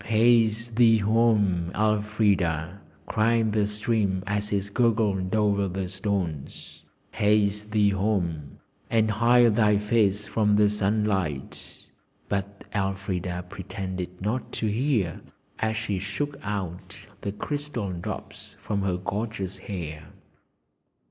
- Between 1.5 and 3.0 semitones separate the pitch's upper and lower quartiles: Yes, narrow, 2.4 semitones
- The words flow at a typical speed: No, slow, 115 wpm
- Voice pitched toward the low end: Yes, low, 105 Hz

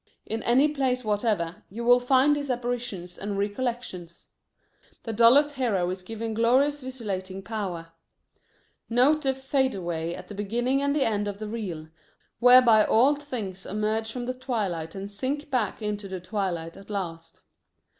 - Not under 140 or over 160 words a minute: Yes, average, 155 wpm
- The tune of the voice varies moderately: Yes, average, 4.7 semitones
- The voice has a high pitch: Yes, high, 225 Hz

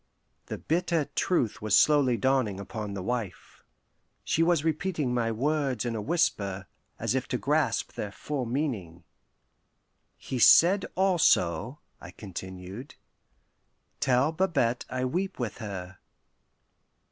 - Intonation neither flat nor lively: No, wide, 6.7 semitones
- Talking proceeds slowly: Yes, slow, 125 wpm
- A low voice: Yes, low, 125 Hz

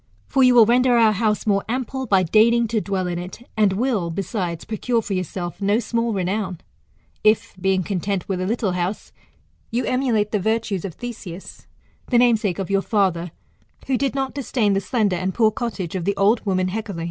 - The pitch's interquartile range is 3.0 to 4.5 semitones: Yes, average, 3.8 semitones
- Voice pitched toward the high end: Yes, high, 205 Hz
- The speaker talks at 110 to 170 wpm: No, average, 195 wpm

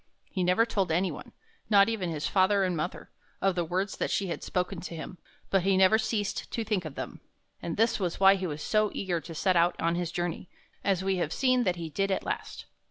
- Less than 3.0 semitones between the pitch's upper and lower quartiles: Yes, narrow, 2.5 semitones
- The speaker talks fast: Yes, fast, 235 wpm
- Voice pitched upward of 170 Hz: Yes, medium, 185 Hz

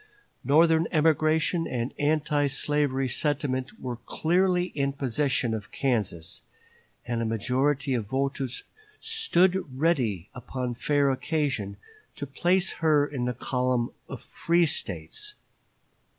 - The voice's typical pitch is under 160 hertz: Yes, medium, 140 Hz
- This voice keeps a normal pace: No, slow, 115 wpm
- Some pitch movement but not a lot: Yes, average, 3.9 semitones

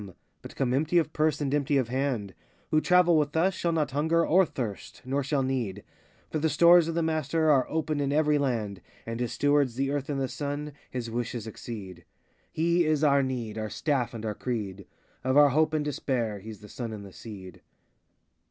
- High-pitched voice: No, medium, 140 Hz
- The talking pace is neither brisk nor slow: No, fast, 210 wpm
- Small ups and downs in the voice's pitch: No, average, 4.9 semitones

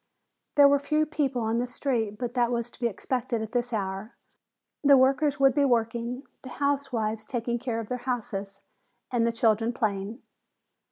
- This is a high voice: Yes, high, 240 Hz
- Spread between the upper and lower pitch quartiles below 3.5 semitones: Yes, average, 2.9 semitones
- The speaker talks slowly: No, average, 175 wpm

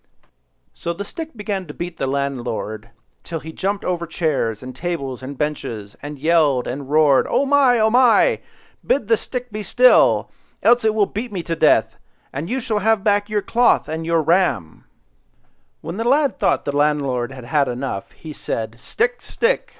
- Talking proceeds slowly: No, average, 180 wpm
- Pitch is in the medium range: Yes, medium, 165 Hz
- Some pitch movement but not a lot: No, wide, 8.0 semitones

